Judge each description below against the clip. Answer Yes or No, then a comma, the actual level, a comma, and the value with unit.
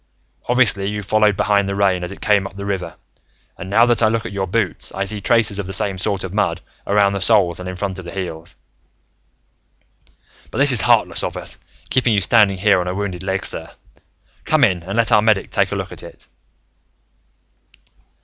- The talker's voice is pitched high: No, low, 100 Hz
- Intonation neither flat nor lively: No, narrow, 2.2 semitones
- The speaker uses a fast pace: Yes, fast, 210 wpm